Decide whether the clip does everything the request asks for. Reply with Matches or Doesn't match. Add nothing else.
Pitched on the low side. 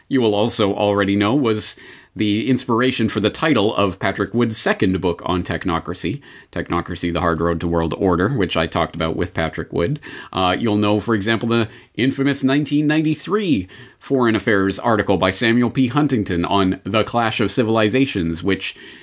Matches